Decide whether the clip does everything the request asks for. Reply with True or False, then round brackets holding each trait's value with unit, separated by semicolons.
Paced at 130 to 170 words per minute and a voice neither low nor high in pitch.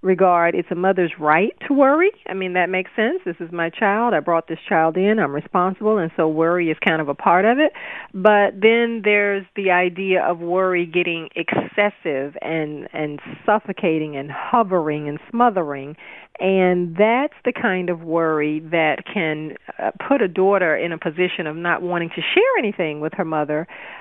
False (180 wpm; 180 Hz)